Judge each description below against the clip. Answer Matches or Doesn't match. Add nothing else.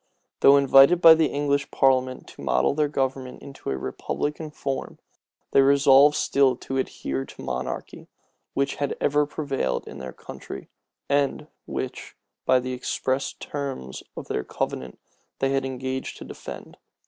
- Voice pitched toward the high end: Doesn't match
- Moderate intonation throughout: Doesn't match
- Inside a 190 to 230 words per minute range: Doesn't match